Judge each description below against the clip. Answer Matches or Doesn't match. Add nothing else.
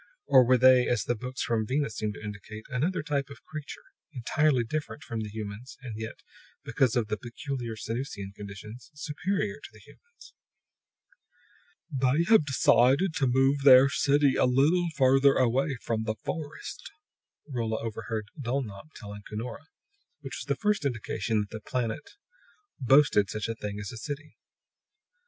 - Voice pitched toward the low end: Matches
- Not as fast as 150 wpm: Doesn't match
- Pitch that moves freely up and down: Doesn't match